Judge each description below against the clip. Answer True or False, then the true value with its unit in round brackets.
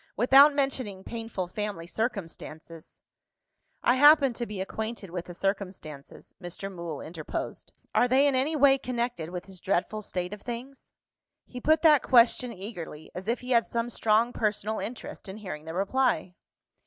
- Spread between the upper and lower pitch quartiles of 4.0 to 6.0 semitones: True (5.5 semitones)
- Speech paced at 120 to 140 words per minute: False (165 wpm)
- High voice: True (215 Hz)